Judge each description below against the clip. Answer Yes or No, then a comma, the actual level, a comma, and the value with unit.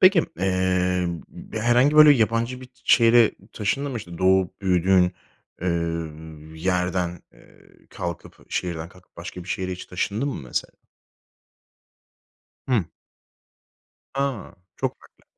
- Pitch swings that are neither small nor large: Yes, average, 5.0 semitones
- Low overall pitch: Yes, very low, 95 Hz